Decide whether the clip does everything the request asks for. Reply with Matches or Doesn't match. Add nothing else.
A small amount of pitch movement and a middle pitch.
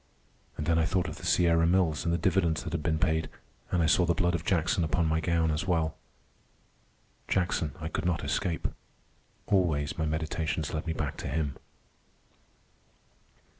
Doesn't match